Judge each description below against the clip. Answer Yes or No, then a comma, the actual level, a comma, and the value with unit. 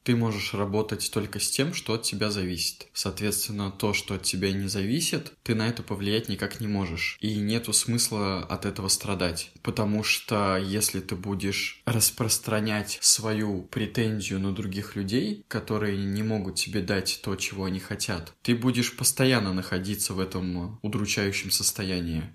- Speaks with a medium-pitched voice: No, low, 105 Hz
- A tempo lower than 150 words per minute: No, average, 155 wpm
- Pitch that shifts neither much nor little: No, narrow, 2.2 semitones